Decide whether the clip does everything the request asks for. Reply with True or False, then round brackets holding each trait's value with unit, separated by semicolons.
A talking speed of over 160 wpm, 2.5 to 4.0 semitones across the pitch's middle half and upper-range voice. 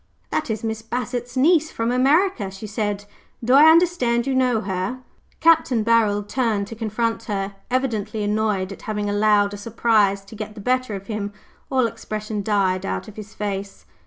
True (175 wpm; 3.3 semitones; 220 Hz)